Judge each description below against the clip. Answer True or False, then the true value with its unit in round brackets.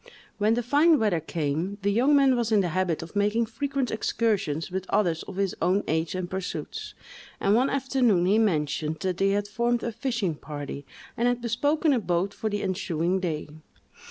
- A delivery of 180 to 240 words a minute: True (190 wpm)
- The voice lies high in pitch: True (200 Hz)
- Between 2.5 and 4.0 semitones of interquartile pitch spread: False (5.2 semitones)